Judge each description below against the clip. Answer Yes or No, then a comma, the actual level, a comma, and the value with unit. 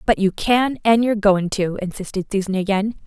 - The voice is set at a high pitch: Yes, high, 205 Hz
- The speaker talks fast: No, average, 195 wpm